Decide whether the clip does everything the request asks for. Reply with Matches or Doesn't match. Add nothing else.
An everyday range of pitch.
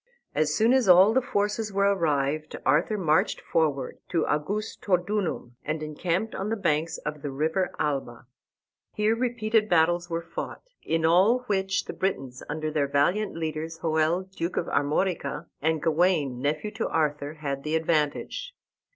Matches